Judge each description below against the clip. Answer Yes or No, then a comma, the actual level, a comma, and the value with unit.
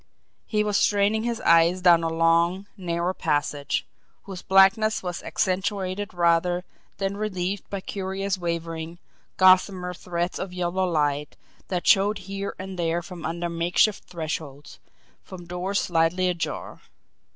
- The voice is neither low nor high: Yes, medium, 180 Hz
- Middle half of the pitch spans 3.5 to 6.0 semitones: No, narrow, 2.4 semitones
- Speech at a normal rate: No, slow, 130 wpm